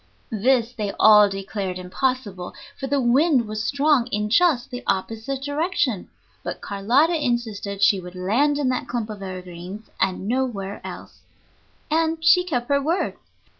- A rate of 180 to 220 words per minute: No, average, 150 wpm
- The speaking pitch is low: No, high, 235 Hz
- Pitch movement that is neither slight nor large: No, wide, 5.8 semitones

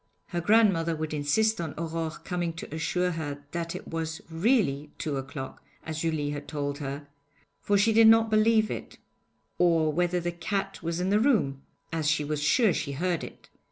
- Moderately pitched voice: Yes, medium, 165 Hz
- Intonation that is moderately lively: Yes, average, 4.4 semitones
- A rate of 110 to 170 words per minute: No, average, 185 wpm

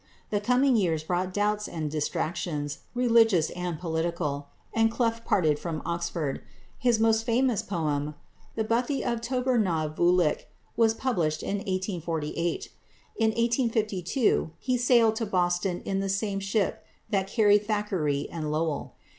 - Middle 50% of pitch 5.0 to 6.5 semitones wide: Yes, wide, 5.5 semitones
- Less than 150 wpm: Yes, average, 140 wpm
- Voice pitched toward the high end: Yes, high, 195 Hz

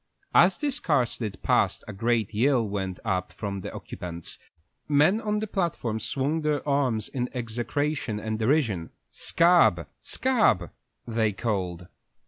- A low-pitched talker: Yes, low, 115 Hz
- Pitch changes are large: Yes, wide, 6.5 semitones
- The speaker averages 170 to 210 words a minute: No, average, 145 wpm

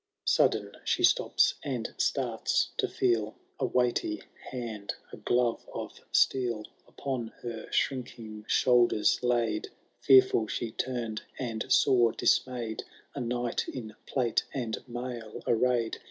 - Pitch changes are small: Yes, narrow, 2.1 semitones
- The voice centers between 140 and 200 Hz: No, low, 120 Hz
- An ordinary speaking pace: No, slow, 120 wpm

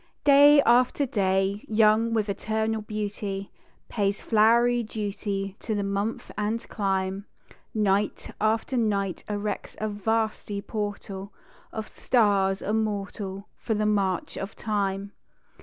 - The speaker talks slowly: Yes, slow, 115 wpm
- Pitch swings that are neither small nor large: No, narrow, 1.8 semitones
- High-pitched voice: Yes, high, 210 Hz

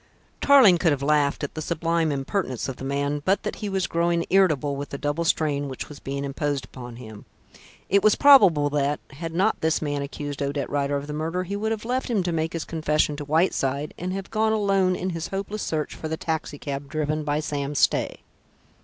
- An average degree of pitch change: Yes, average, 4.3 semitones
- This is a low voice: No, medium, 155 Hz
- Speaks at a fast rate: Yes, fast, 215 wpm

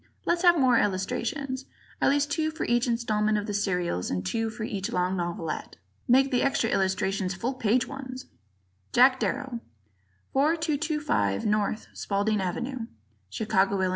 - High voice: Yes, high, 230 Hz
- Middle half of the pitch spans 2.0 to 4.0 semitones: No, wide, 5.6 semitones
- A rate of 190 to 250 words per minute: No, average, 145 wpm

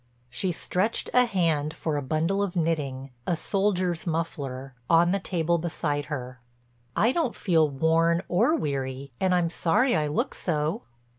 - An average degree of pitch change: Yes, average, 3.8 semitones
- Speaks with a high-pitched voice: No, medium, 165 Hz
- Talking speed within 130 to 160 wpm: Yes, average, 145 wpm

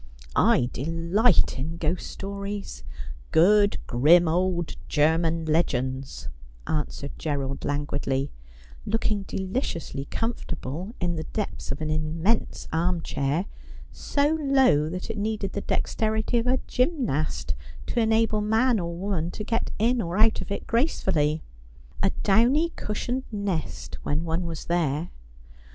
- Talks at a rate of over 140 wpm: No, slow, 135 wpm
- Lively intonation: Yes, wide, 5.9 semitones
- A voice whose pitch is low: No, medium, 175 Hz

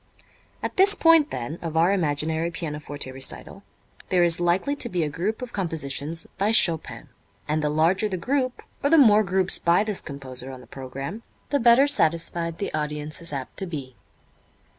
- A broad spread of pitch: Yes, wide, 5.7 semitones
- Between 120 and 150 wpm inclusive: No, average, 180 wpm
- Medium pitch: Yes, medium, 170 Hz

